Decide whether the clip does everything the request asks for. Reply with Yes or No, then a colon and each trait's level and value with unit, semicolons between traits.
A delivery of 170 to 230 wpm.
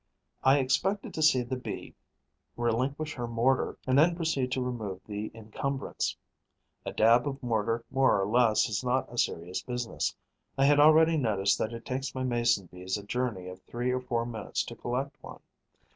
Yes: average, 180 wpm